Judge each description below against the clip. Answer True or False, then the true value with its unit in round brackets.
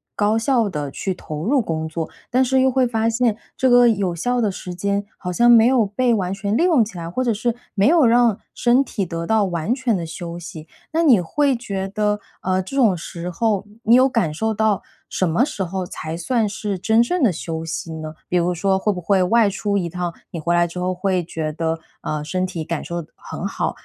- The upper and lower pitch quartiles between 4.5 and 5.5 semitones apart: True (5.2 semitones)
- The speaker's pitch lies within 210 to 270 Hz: False (200 Hz)